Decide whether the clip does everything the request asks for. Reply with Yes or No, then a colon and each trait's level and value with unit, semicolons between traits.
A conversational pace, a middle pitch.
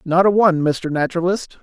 Yes: average, 185 wpm; medium, 175 Hz